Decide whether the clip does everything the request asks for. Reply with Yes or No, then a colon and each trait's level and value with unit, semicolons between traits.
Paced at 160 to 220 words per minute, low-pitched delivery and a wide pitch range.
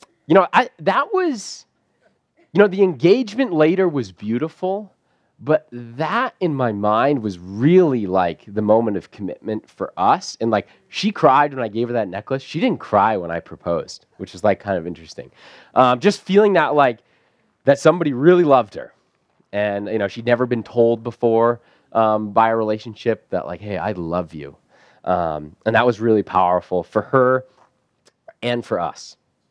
Yes: average, 175 wpm; low, 120 Hz; wide, 7.3 semitones